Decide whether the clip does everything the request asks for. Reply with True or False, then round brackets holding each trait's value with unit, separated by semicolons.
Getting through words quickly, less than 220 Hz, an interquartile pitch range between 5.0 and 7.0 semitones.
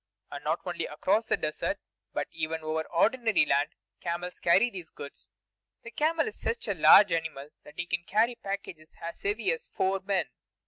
False (180 wpm; 185 Hz; 5.6 semitones)